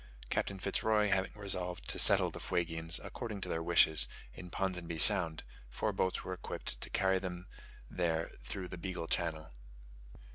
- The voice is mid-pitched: No, very low, 90 Hz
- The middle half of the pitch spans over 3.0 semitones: No, narrow, 2.6 semitones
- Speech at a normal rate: Yes, average, 160 wpm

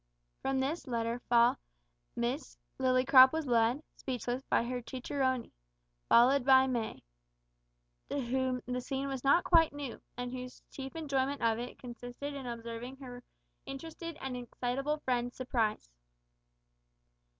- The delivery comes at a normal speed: No, slow, 130 wpm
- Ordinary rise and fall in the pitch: No, narrow, 2.0 semitones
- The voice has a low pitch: No, very high, 255 Hz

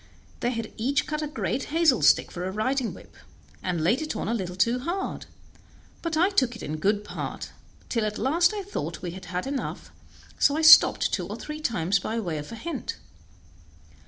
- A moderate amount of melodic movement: No, wide, 7.8 semitones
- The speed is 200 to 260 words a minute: Yes, fast, 205 wpm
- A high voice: Yes, high, 240 Hz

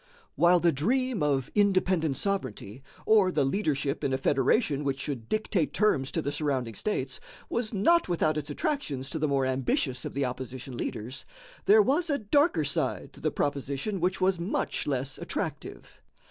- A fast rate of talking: No, average, 170 wpm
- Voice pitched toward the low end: No, medium, 150 Hz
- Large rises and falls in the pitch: Yes, wide, 7.0 semitones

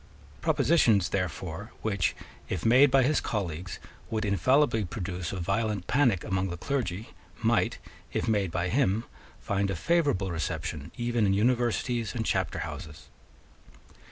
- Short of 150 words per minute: Yes, slow, 135 wpm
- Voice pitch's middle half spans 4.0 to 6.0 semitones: Yes, average, 4.6 semitones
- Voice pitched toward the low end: Yes, low, 105 Hz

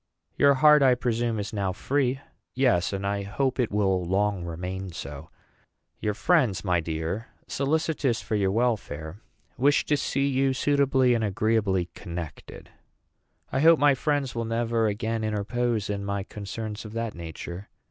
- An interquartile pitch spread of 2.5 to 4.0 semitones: No, average, 5.2 semitones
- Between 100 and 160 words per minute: Yes, average, 155 wpm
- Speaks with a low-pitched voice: Yes, low, 110 Hz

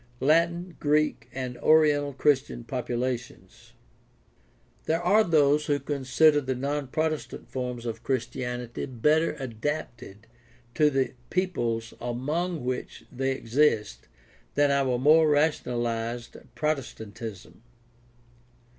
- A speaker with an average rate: No, slow, 105 wpm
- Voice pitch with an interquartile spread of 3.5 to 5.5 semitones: Yes, average, 3.9 semitones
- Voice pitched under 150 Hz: Yes, low, 135 Hz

